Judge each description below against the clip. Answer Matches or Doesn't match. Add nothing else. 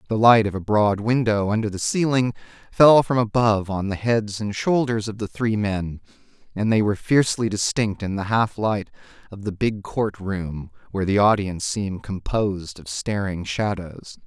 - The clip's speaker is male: Matches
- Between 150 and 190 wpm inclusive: Matches